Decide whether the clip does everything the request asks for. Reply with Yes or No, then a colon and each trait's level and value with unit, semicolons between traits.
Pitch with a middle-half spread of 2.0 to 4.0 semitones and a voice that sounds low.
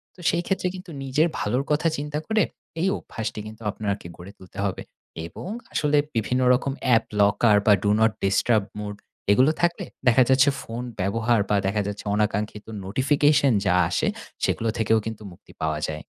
No: average, 5.2 semitones; low, 110 Hz